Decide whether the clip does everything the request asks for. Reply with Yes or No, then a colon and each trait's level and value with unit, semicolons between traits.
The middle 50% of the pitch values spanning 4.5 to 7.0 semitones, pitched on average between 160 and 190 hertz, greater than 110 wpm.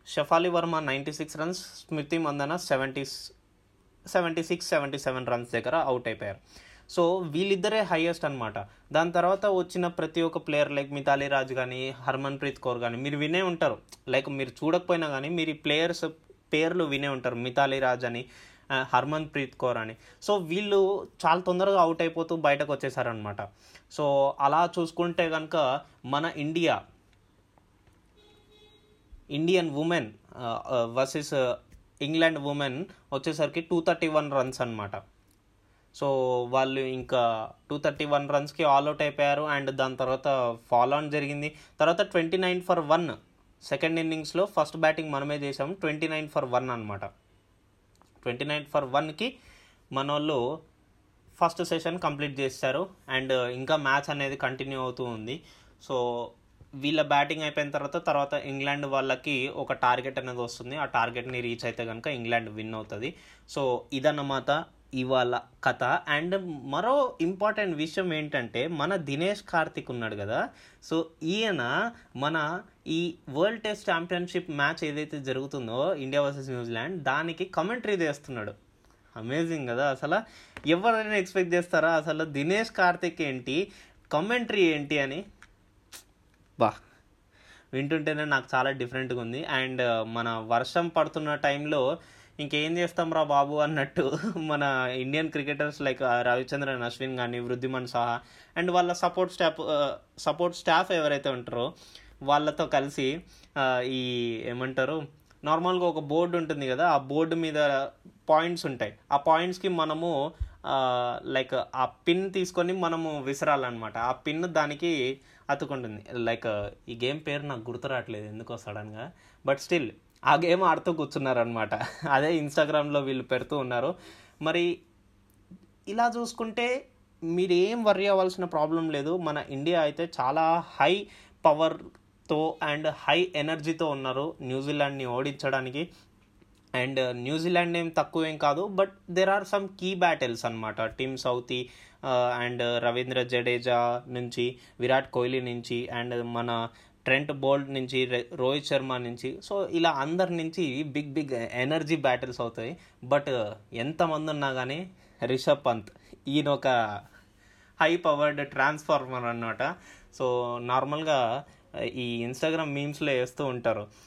No: average, 4.8 semitones; medium, 140 Hz; fast, 125 wpm